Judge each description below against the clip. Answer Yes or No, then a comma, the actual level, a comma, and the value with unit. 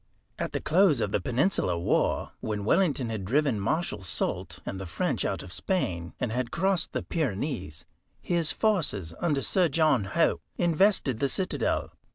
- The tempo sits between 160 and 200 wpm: Yes, average, 165 wpm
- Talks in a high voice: No, low, 135 Hz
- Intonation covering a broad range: Yes, wide, 8.9 semitones